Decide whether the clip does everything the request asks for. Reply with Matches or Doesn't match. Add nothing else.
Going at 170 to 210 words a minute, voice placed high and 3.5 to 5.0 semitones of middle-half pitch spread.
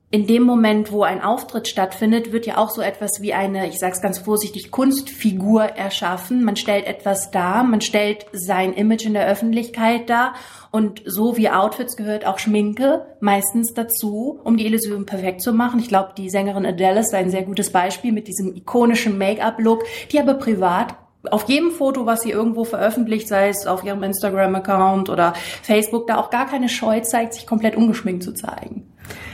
Doesn't match